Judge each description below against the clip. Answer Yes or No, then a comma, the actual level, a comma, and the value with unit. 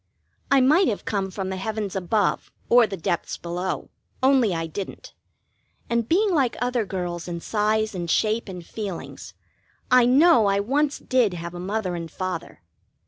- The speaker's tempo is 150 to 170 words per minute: Yes, average, 165 wpm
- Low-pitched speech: No, high, 205 Hz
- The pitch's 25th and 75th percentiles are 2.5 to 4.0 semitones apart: No, average, 5.1 semitones